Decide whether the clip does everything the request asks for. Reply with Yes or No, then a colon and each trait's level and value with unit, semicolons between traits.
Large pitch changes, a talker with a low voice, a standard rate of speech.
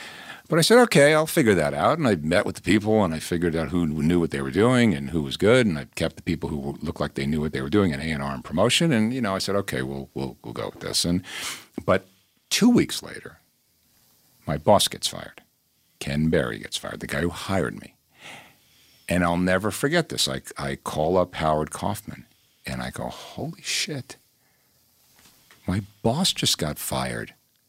No: wide, 5.7 semitones; very low, 85 Hz; fast, 210 wpm